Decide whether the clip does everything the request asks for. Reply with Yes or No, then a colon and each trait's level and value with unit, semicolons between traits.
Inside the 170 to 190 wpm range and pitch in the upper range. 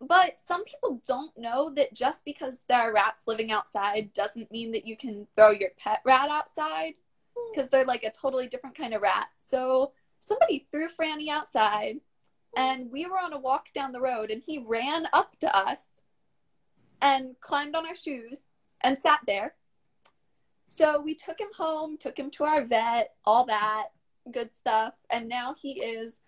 Yes: average, 180 wpm; very high, 265 Hz